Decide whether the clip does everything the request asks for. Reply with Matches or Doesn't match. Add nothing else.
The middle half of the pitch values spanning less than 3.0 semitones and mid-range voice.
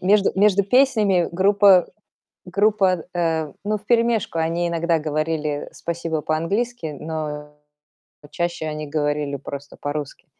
Doesn't match